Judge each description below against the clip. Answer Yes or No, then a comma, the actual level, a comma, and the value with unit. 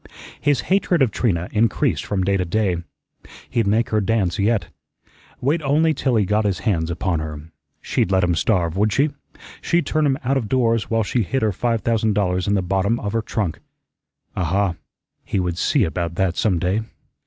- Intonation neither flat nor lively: Yes, average, 4.4 semitones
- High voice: No, low, 105 Hz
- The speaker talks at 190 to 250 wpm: Yes, average, 195 wpm